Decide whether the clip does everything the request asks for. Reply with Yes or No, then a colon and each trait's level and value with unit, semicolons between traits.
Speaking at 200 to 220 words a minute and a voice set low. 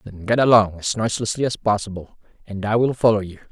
Yes: fast, 205 wpm; low, 110 Hz